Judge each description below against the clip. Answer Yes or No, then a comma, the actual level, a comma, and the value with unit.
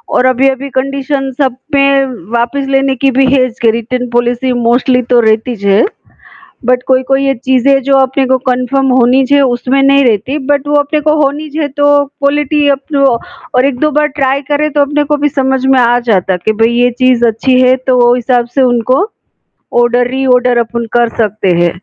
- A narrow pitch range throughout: Yes, narrow, 2.2 semitones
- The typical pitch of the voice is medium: No, very high, 260 Hz